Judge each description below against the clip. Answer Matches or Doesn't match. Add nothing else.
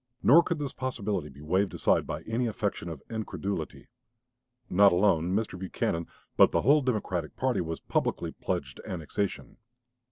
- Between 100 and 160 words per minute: Matches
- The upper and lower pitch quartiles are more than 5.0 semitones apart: Matches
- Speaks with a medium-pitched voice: Doesn't match